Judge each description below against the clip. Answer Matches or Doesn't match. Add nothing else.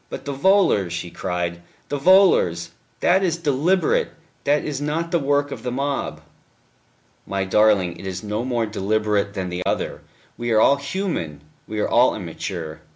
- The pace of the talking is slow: Doesn't match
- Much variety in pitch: Matches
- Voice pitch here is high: Doesn't match